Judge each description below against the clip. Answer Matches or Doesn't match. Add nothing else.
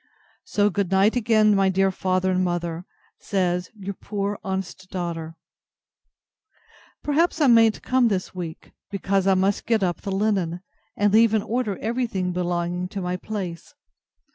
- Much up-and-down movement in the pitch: Doesn't match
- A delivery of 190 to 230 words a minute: Doesn't match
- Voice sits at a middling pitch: Doesn't match